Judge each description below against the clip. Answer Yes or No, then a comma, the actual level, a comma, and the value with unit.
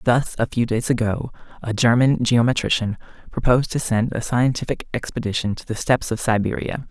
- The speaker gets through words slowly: No, average, 165 wpm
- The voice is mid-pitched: No, low, 115 Hz